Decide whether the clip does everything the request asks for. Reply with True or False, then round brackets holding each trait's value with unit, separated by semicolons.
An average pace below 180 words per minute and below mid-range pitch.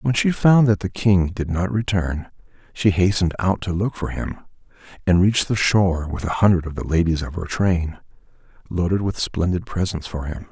False (200 wpm; 90 Hz)